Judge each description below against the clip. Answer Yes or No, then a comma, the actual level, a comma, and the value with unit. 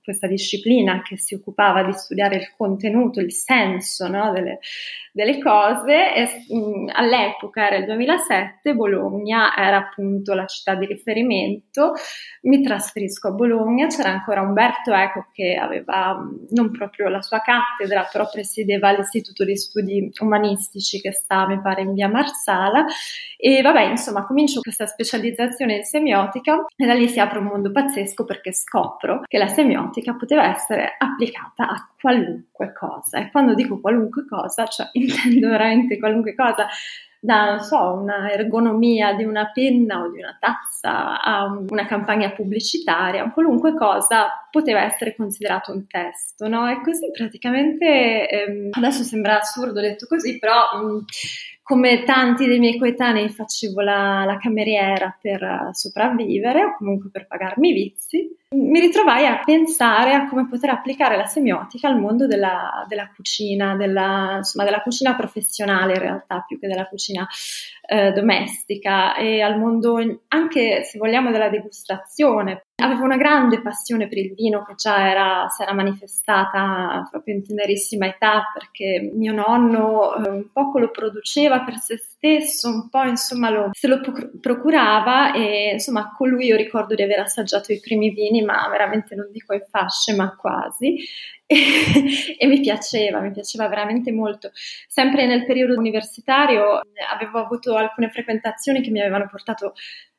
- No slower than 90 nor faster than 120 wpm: No, average, 150 wpm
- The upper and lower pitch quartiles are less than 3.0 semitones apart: No, average, 4.0 semitones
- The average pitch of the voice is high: Yes, high, 220 Hz